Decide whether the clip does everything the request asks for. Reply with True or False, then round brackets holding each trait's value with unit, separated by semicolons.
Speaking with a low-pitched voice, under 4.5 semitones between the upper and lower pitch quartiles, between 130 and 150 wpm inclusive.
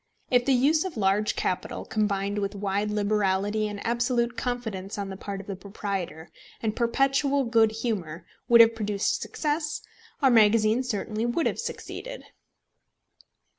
False (215 Hz; 3.4 semitones; 145 wpm)